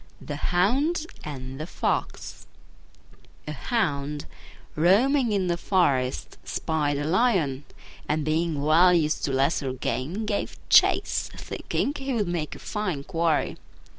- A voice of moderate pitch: Yes, medium, 165 Hz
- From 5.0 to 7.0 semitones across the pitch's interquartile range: Yes, wide, 5.6 semitones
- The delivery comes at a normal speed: No, slow, 130 wpm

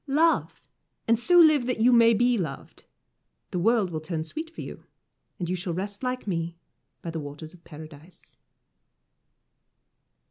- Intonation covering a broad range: Yes, wide, 7.0 semitones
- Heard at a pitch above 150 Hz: Yes, high, 190 Hz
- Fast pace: No, average, 155 wpm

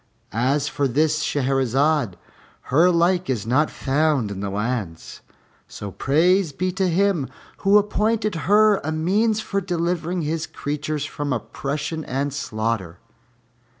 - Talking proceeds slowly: Yes, slow, 130 wpm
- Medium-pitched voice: Yes, medium, 150 Hz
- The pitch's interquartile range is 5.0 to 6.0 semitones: Yes, wide, 5.5 semitones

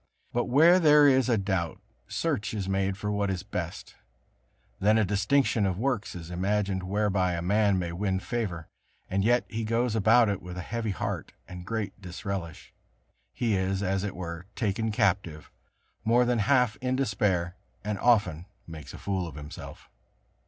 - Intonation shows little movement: No, average, 3.5 semitones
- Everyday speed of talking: Yes, average, 170 wpm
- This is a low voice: Yes, low, 100 Hz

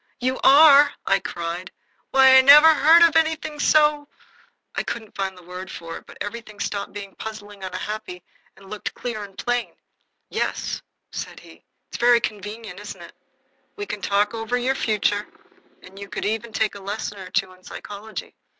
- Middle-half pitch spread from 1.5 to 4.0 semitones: No, average, 4.9 semitones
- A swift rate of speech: No, average, 180 wpm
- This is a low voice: No, high, 215 Hz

